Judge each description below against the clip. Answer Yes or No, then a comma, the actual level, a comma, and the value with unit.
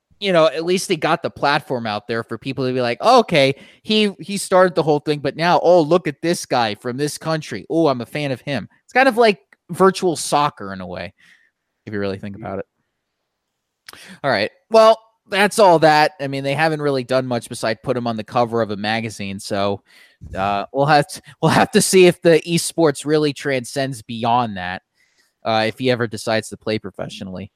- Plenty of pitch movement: Yes, wide, 7.0 semitones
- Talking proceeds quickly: Yes, fast, 220 wpm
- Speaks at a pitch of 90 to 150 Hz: Yes, medium, 140 Hz